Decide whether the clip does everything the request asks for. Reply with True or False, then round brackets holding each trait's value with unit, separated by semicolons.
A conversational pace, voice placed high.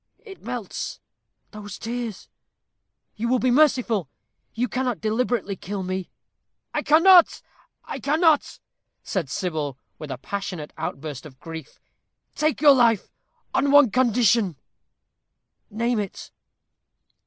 False (115 wpm; 225 Hz)